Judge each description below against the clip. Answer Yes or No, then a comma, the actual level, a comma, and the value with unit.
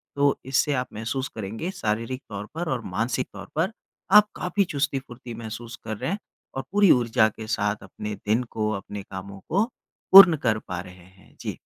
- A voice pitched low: Yes, low, 115 Hz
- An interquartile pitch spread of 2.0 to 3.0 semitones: No, average, 5.2 semitones